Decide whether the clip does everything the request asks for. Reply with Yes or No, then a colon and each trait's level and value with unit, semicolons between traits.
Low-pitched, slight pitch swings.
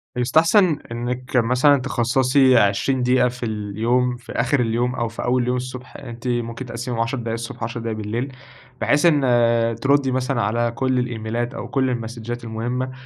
Yes: low, 120 Hz; narrow, 1.9 semitones